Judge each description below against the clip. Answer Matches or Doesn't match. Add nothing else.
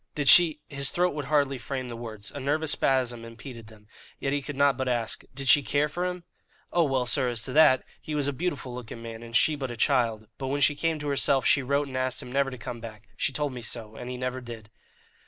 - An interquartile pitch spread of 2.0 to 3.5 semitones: Matches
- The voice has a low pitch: Matches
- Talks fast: Matches